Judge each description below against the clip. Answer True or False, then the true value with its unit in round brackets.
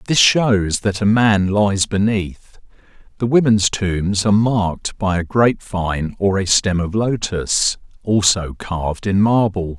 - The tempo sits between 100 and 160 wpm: True (145 wpm)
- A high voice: False (100 Hz)